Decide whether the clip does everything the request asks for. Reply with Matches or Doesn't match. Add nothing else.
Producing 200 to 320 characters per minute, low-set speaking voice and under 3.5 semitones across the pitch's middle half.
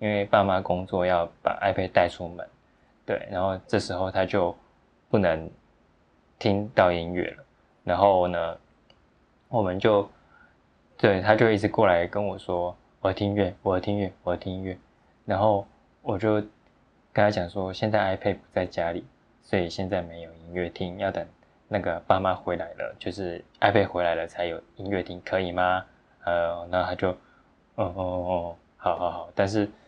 Matches